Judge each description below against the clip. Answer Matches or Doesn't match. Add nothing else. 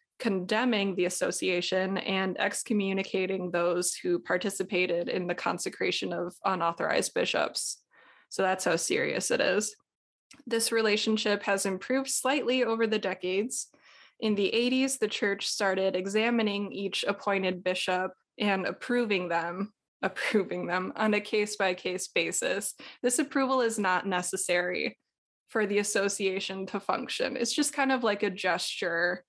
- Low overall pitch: Doesn't match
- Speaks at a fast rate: Doesn't match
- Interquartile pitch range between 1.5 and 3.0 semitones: Doesn't match